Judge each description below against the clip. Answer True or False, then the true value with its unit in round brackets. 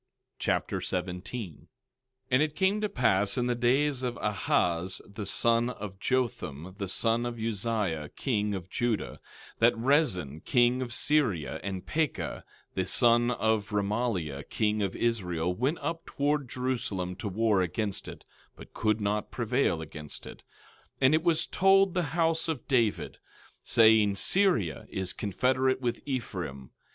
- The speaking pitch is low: True (115 Hz)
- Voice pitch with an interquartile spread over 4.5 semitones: True (5.2 semitones)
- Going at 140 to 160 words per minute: True (155 wpm)